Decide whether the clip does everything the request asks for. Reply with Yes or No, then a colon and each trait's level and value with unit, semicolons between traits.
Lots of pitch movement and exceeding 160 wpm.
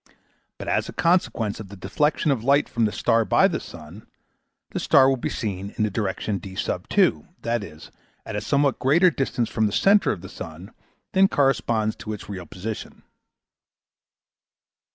Yes: wide, 5.7 semitones; average, 170 wpm